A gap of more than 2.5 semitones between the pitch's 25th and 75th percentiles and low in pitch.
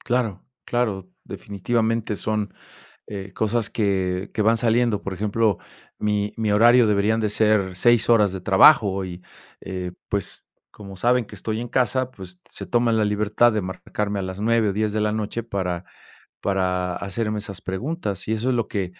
Yes: average, 2.9 semitones; low, 105 Hz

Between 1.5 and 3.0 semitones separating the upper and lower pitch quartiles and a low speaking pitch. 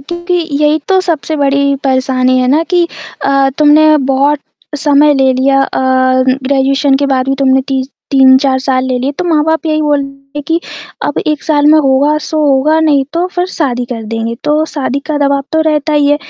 No: narrow, 2.4 semitones; very high, 280 Hz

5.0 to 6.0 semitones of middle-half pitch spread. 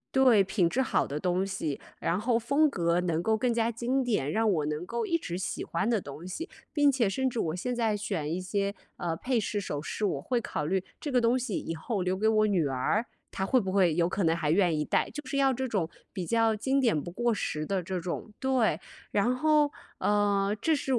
Yes: wide, 5.5 semitones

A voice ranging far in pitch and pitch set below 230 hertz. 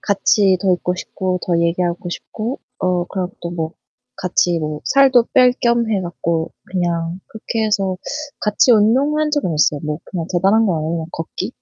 No: average, 4.5 semitones; medium, 185 Hz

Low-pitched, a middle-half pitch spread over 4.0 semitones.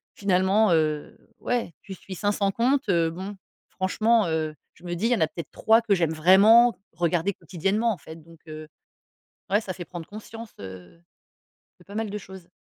No: high, 190 Hz; average, 4.4 semitones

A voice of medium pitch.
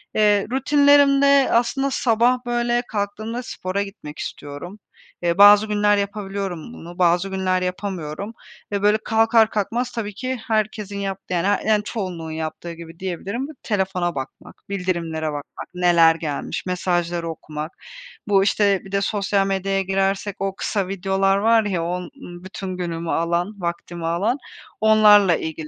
No: high, 195 Hz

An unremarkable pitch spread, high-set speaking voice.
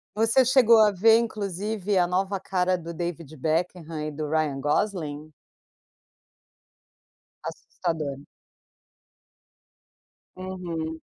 No: average, 4.4 semitones; medium, 180 Hz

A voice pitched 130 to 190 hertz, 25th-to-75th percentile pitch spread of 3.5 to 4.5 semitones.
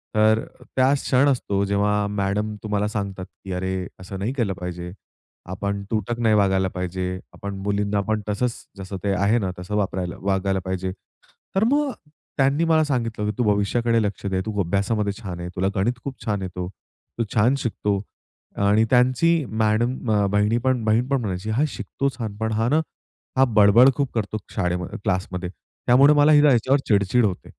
No: low, 105 Hz; average, 3.8 semitones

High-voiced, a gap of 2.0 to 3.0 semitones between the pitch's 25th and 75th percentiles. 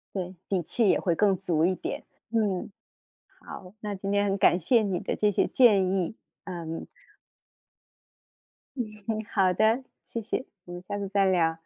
Yes: high, 195 Hz; average, 2.7 semitones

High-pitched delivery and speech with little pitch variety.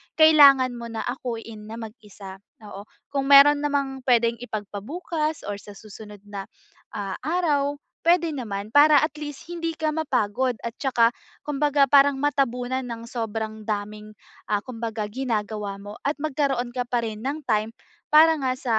No: high, 245 Hz; average, 5.0 semitones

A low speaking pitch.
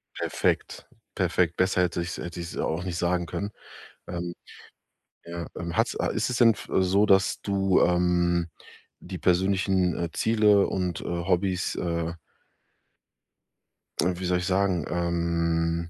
Yes: very low, 90 Hz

